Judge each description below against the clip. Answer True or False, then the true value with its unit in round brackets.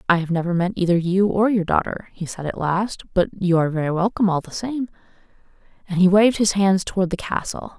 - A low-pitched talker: False (190 Hz)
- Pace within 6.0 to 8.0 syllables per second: True (6.1 syllables/s)